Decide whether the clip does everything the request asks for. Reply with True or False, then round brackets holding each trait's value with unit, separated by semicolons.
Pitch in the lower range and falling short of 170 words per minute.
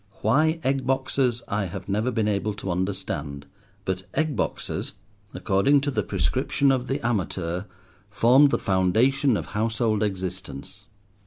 True (105 Hz; 140 wpm)